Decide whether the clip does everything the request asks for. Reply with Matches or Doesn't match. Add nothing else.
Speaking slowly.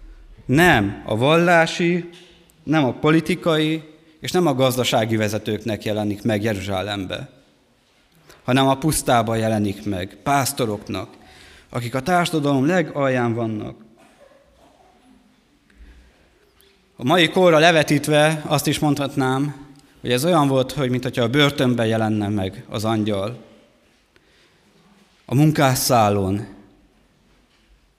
Matches